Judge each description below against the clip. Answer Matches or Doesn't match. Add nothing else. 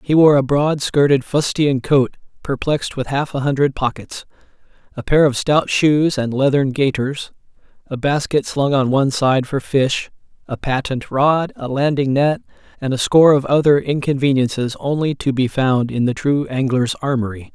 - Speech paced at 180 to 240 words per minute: Doesn't match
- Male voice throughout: Matches